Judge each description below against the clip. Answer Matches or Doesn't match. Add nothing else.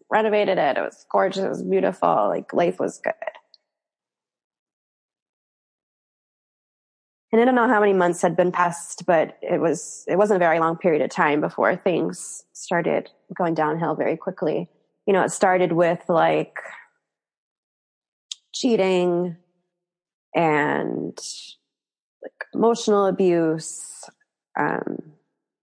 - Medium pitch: Matches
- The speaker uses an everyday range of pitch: Matches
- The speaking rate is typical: Doesn't match